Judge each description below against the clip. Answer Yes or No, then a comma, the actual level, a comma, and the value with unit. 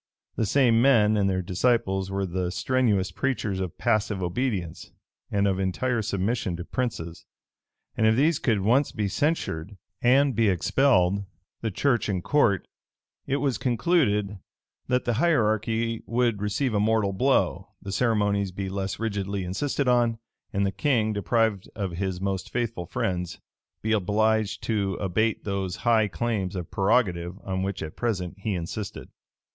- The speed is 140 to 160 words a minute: Yes, average, 150 wpm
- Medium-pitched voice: No, low, 105 Hz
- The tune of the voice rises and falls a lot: No, average, 3.7 semitones